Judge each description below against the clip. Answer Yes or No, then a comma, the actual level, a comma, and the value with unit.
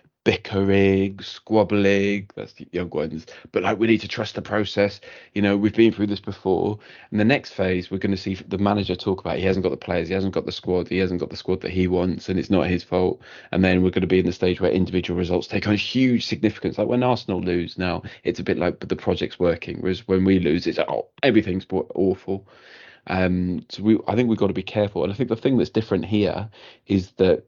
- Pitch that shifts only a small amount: Yes, narrow, 2.3 semitones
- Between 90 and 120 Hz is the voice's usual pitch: Yes, very low, 95 Hz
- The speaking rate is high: Yes, fast, 250 wpm